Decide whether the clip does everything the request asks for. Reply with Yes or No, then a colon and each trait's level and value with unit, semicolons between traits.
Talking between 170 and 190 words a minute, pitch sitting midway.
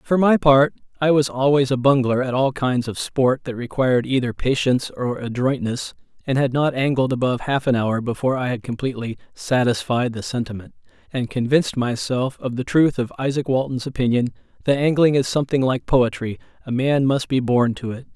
No: average, 185 wpm; low, 130 Hz